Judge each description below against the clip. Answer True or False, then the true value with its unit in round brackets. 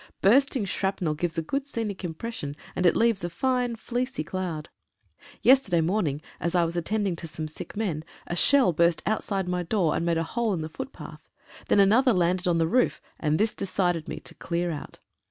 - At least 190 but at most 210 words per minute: True (195 wpm)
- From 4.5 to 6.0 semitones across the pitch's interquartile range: True (4.9 semitones)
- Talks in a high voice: False (180 Hz)